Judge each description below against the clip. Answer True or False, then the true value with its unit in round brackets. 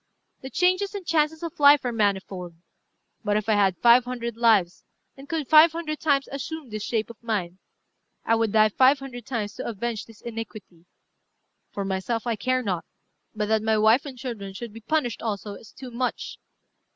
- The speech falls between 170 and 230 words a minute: True (190 wpm)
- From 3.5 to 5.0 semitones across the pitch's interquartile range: True (4.4 semitones)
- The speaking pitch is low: False (230 Hz)